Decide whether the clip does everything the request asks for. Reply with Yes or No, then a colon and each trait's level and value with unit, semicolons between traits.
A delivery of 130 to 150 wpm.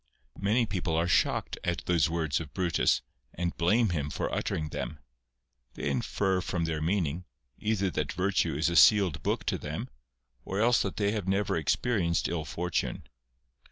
No: average, 165 wpm